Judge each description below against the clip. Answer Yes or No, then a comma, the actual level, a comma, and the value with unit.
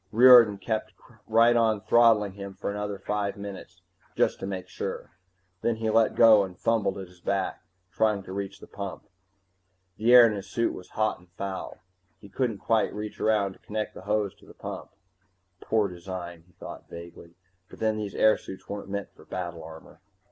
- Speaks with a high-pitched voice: No, low, 100 Hz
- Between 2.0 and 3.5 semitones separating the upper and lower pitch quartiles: Yes, narrow, 2.5 semitones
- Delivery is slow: No, average, 185 wpm